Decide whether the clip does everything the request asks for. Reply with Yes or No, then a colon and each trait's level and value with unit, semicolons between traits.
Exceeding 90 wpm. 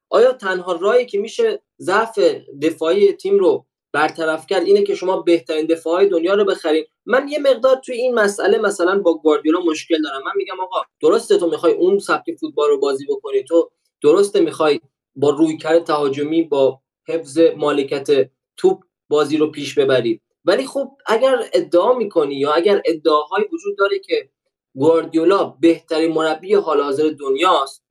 Yes: fast, 155 wpm